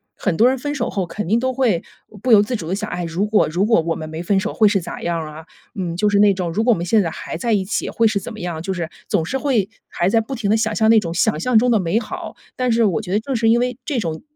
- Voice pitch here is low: No, high, 205 Hz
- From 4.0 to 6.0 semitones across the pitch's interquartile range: Yes, average, 4.7 semitones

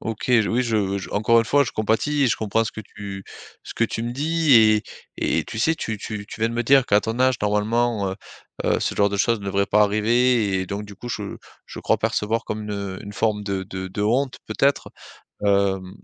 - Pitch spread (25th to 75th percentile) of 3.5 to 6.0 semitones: No, average, 2.7 semitones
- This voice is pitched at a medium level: No, low, 110 Hz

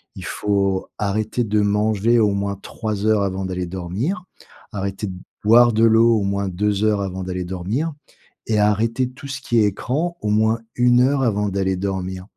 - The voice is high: No, low, 105 Hz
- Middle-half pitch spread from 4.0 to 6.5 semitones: No, average, 2.9 semitones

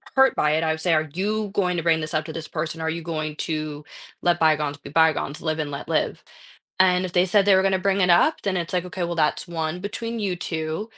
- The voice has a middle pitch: Yes, medium, 170 Hz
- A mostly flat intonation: No, average, 3.1 semitones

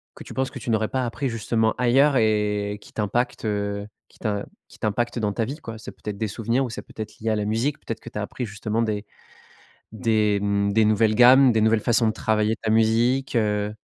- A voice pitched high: No, low, 110 Hz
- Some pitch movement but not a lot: No, narrow, 2.2 semitones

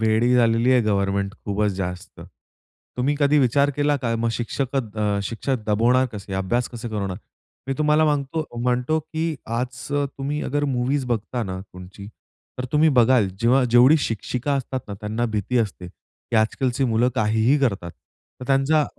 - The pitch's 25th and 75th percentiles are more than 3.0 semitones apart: Yes, average, 4.2 semitones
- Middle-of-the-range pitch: No, low, 120 Hz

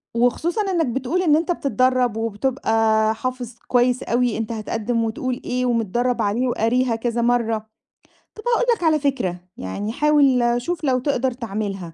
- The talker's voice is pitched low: No, high, 245 Hz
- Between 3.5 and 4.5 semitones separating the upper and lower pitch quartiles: No, average, 2.9 semitones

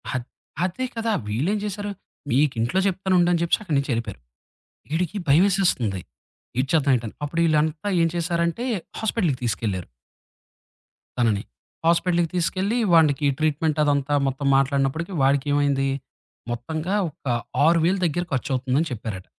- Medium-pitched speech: Yes, medium, 155 Hz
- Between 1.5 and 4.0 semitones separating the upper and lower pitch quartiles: No, average, 4.5 semitones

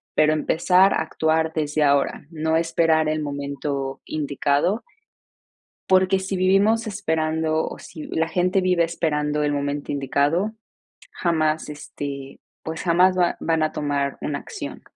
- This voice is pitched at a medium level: Yes, medium, 160 Hz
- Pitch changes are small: No, average, 3.2 semitones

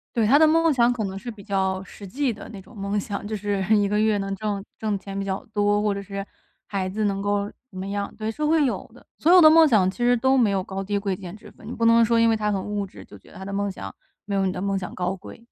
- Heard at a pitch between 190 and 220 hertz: Yes, high, 205 Hz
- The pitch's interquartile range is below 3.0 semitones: Yes, narrow, 2.6 semitones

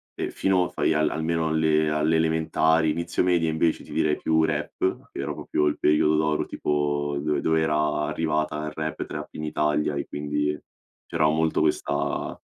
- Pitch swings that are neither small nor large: No, narrow, 1.1 semitones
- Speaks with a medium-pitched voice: No, very low, 75 Hz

